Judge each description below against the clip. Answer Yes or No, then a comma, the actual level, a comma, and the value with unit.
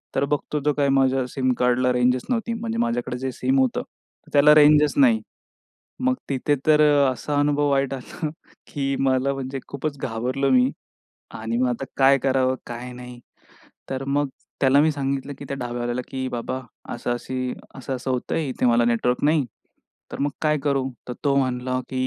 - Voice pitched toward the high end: No, low, 135 Hz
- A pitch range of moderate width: No, narrow, 2.3 semitones